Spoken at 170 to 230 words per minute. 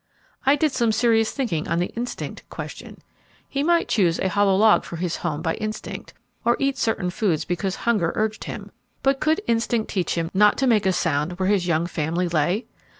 Yes: average, 200 wpm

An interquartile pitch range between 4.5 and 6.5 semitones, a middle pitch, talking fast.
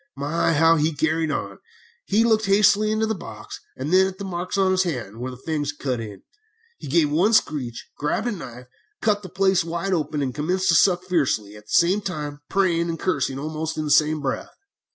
Yes: average, 4.8 semitones; medium, 165 Hz; fast, 220 wpm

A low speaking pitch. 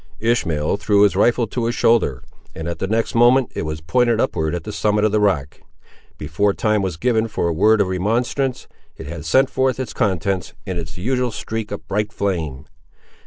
Yes: low, 105 Hz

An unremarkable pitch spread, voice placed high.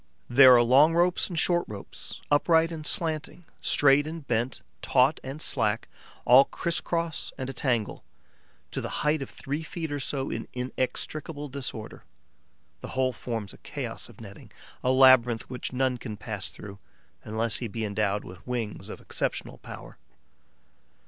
No: average, 4.6 semitones; low, 130 Hz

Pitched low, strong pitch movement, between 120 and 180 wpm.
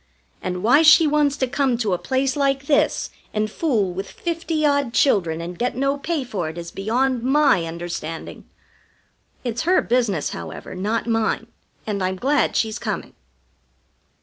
No: high, 240 Hz; wide, 6.6 semitones; average, 160 wpm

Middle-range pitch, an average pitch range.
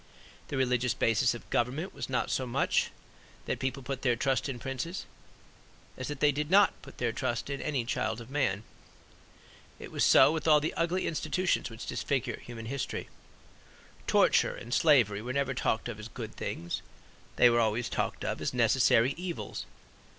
No: low, 130 Hz; average, 3.8 semitones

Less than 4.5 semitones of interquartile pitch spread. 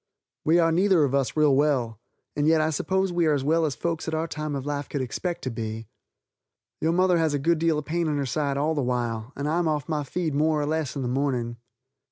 Yes: average, 2.9 semitones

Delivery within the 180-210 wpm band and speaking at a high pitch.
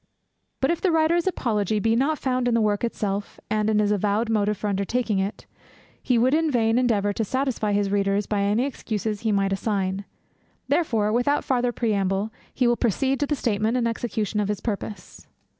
Yes: average, 190 wpm; high, 220 Hz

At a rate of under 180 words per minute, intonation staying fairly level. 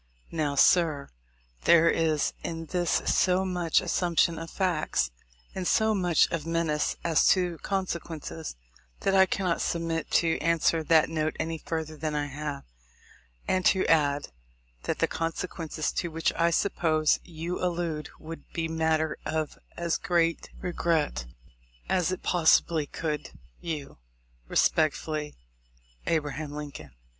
Yes: average, 140 wpm; narrow, 1.9 semitones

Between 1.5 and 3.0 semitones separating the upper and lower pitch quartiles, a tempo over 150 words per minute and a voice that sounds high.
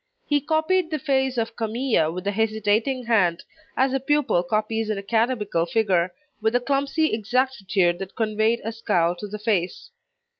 No: average, 4.8 semitones; average, 160 wpm; high, 225 Hz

